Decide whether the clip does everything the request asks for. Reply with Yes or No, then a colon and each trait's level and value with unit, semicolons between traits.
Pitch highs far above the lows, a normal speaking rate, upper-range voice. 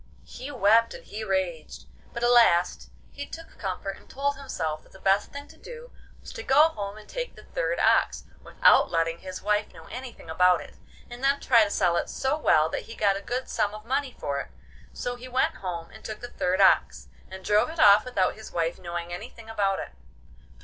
No: wide, 5.7 semitones; fast, 220 wpm; high, 210 Hz